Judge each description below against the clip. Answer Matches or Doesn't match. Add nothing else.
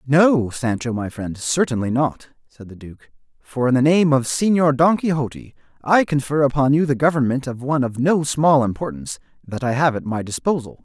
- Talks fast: Doesn't match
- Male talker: Matches